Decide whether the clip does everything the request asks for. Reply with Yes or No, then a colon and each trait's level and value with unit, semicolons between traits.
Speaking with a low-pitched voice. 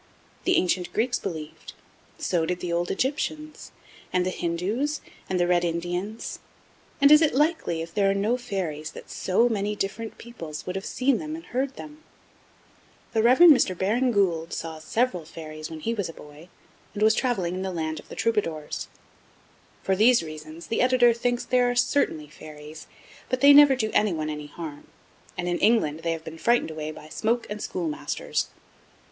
No: high, 190 Hz